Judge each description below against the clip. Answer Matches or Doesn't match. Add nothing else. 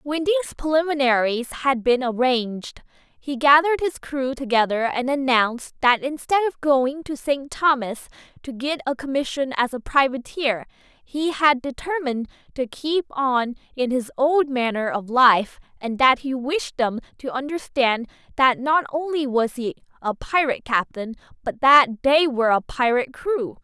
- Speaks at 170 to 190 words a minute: Doesn't match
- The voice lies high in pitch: Matches